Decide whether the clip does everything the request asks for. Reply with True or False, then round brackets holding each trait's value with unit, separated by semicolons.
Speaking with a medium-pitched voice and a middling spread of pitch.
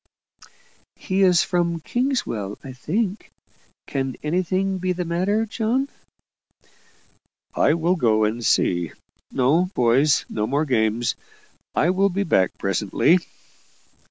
False (170 Hz; 7.7 semitones)